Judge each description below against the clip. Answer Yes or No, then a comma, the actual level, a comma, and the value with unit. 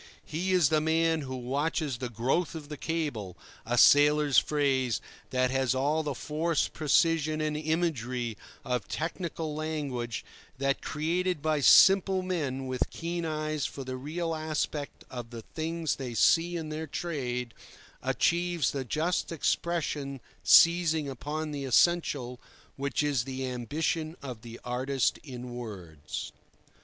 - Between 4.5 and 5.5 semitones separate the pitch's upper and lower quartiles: No, average, 3.9 semitones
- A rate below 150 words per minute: Yes, slow, 135 wpm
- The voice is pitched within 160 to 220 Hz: No, medium, 150 Hz